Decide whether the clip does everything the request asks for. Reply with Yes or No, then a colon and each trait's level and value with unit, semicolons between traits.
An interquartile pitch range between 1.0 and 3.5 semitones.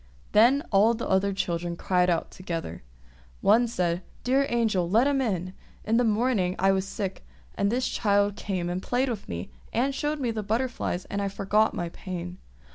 No: average, 4.5 semitones